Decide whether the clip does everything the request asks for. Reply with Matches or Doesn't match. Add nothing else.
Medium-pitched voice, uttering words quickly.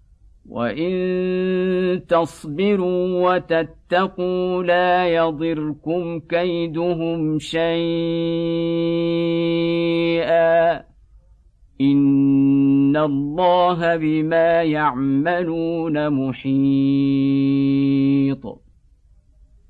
Doesn't match